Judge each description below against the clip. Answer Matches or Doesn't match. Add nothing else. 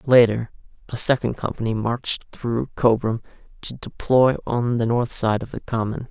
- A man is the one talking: Matches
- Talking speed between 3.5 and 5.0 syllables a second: Matches